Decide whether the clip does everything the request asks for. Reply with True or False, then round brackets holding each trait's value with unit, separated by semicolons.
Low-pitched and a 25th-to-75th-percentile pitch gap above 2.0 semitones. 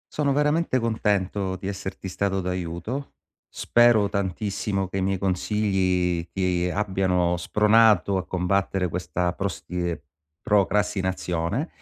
True (95 Hz; 2.5 semitones)